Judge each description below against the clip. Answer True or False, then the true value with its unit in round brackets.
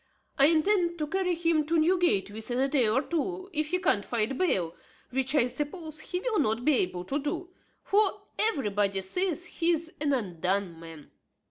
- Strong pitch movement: True (8.4 semitones)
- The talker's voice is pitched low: False (300 Hz)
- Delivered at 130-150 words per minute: False (185 wpm)